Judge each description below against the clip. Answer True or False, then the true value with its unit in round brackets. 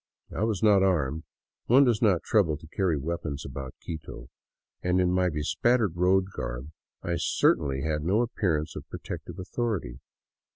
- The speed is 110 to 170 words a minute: True (165 wpm)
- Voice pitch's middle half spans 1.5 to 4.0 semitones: False (4.8 semitones)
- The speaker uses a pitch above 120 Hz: False (90 Hz)